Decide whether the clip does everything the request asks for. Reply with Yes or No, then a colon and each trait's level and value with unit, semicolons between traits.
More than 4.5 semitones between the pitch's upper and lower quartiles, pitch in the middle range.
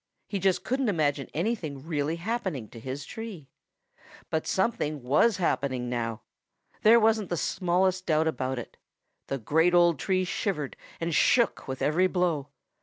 Yes: average, 5.2 semitones; medium, 165 Hz